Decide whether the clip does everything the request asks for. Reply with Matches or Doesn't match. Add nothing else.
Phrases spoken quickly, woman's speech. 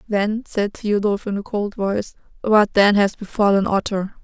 Doesn't match